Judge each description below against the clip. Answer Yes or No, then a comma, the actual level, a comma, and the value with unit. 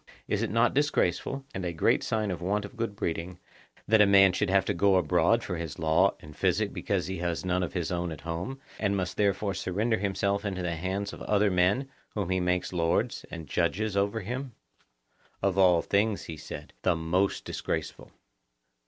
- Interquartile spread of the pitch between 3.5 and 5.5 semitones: No, average, 2.7 semitones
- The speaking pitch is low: Yes, very low, 95 Hz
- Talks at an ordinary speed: Yes, average, 195 wpm